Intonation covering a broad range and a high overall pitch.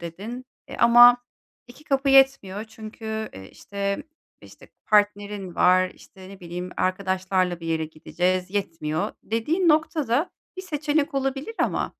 Yes: wide, 6.6 semitones; high, 210 Hz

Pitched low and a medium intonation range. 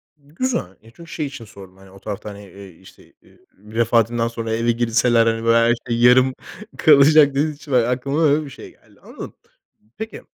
Yes: low, 120 Hz; average, 4.1 semitones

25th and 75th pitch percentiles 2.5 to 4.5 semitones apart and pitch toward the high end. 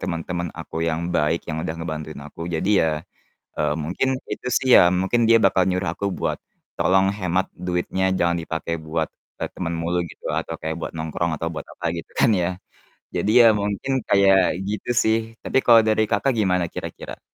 No: average, 3.3 semitones; very low, 90 Hz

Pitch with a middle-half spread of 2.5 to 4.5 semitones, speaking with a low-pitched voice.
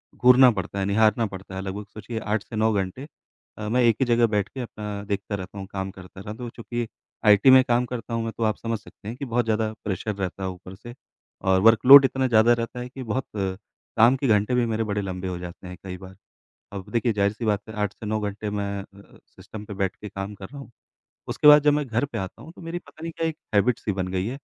Yes: average, 3.4 semitones; low, 110 Hz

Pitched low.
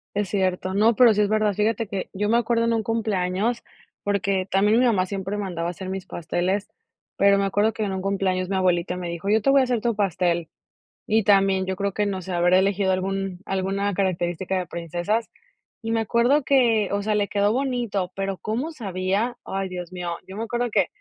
No: high, 195 Hz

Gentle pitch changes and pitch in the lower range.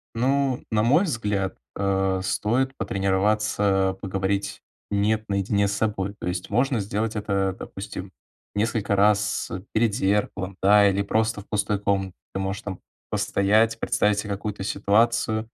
Yes: narrow, 1.9 semitones; low, 105 Hz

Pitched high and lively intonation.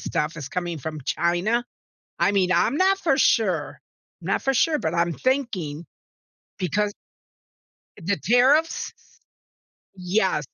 Yes: high, 195 Hz; wide, 6.4 semitones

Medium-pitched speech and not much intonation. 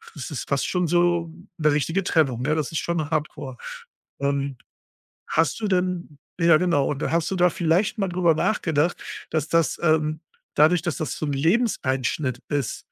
No: medium, 160 Hz; average, 3.2 semitones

